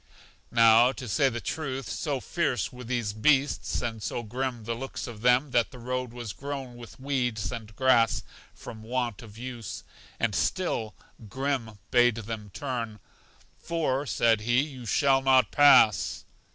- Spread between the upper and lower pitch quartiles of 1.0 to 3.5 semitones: Yes, average, 2.8 semitones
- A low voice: Yes, low, 120 Hz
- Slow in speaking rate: No, average, 155 wpm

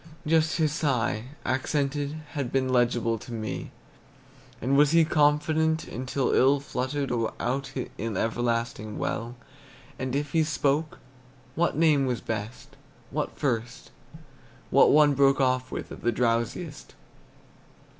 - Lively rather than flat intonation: No, average, 3.6 semitones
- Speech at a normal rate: No, slow, 125 wpm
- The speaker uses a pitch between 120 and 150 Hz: Yes, low, 135 Hz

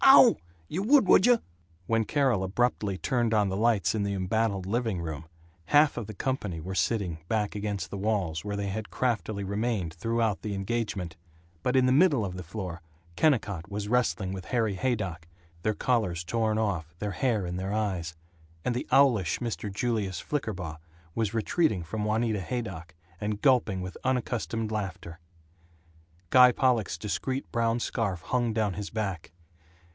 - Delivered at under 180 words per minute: Yes, average, 165 wpm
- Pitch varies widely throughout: No, average, 3.9 semitones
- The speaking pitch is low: Yes, low, 105 Hz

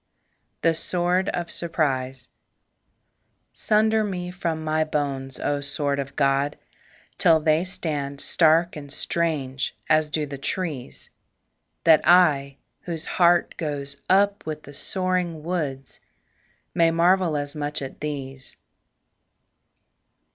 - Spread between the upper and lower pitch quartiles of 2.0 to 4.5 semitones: Yes, average, 3.6 semitones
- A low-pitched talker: No, medium, 155 Hz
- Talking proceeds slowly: Yes, slow, 115 wpm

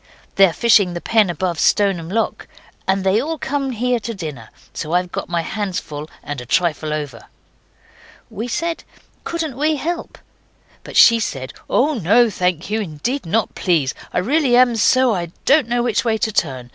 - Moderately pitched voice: No, high, 205 Hz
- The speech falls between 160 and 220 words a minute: Yes, average, 180 wpm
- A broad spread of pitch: Yes, wide, 6.4 semitones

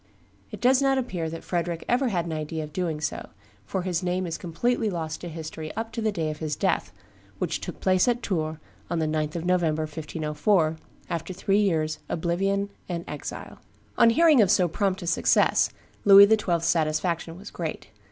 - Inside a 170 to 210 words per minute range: Yes, average, 190 wpm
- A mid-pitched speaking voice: Yes, medium, 175 Hz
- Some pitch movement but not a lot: Yes, average, 3.8 semitones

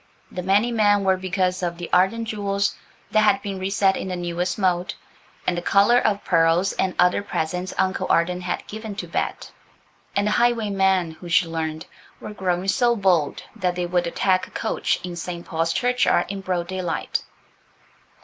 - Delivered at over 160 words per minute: Yes, average, 180 wpm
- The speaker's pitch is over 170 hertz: Yes, medium, 185 Hz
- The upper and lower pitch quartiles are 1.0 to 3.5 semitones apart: Yes, narrow, 2.4 semitones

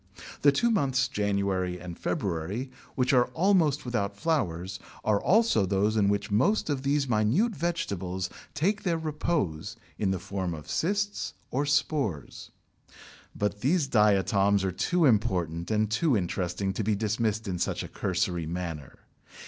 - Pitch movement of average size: No, wide, 7.2 semitones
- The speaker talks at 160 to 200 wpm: No, average, 150 wpm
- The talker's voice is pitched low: Yes, low, 105 Hz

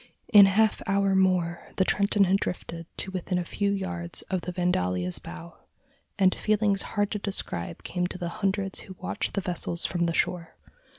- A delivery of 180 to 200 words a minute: Yes, average, 185 wpm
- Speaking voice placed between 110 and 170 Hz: No, medium, 185 Hz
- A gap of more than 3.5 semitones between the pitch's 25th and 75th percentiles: No, narrow, 2.5 semitones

